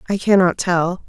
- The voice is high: No, medium, 180 Hz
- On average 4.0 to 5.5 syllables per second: Yes, 4.6 syllables/s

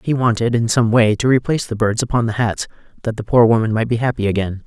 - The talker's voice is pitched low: Yes, low, 115 Hz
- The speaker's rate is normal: No, fast, 255 wpm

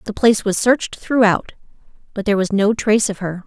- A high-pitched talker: Yes, high, 210 Hz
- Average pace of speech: No, fast, 210 wpm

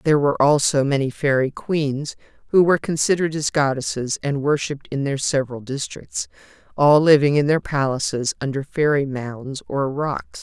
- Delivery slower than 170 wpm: Yes, average, 155 wpm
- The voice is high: No, medium, 140 Hz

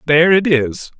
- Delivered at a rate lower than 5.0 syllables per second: No, 5.1 syllables/s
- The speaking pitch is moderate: Yes, medium, 155 Hz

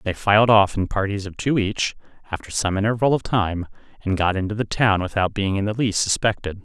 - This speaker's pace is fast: Yes, fast, 215 wpm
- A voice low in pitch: Yes, low, 100 Hz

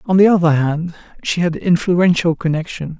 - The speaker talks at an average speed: Yes, average, 160 wpm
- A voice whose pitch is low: No, medium, 170 Hz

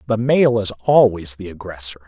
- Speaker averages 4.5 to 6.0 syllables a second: Yes, 4.9 syllables/s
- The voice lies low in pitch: Yes, low, 105 Hz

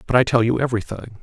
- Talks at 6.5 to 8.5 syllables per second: Yes, 7.3 syllables/s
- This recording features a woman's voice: No, male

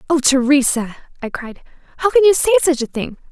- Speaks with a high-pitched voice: Yes, very high, 290 Hz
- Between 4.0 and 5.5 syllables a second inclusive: No, 5.8 syllables/s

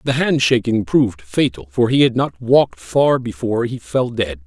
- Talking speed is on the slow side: No, average, 200 wpm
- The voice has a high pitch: No, low, 115 Hz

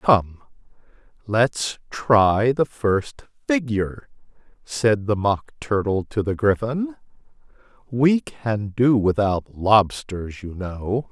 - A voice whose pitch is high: No, low, 110 Hz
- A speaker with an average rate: No, slow, 110 wpm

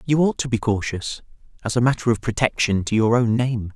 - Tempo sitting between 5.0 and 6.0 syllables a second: Yes, 5.6 syllables/s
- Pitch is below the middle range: Yes, low, 115 Hz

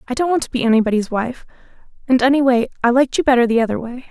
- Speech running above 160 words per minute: Yes, fast, 205 wpm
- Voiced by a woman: Yes, female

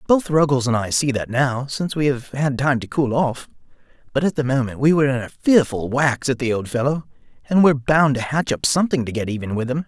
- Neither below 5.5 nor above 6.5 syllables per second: Yes, 6.0 syllables/s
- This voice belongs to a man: Yes, male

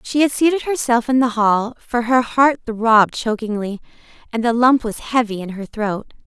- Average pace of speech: Yes, average, 190 wpm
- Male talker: No, female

